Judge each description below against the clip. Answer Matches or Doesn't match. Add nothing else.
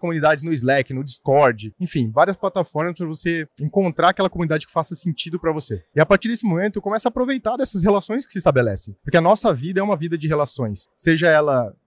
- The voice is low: Doesn't match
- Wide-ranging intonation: Doesn't match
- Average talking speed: Doesn't match